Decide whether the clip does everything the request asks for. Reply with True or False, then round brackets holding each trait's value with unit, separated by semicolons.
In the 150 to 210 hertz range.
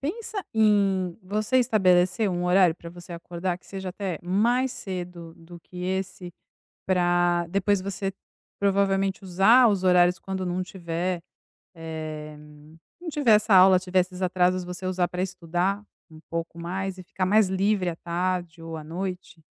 True (185 Hz)